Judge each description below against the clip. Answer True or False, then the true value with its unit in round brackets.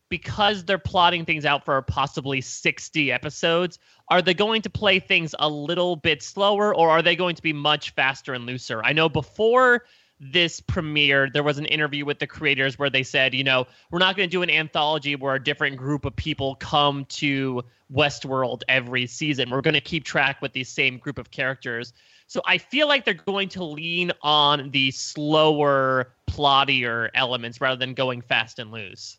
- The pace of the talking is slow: False (195 wpm)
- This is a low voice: False (145 Hz)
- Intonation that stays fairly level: False (4.2 semitones)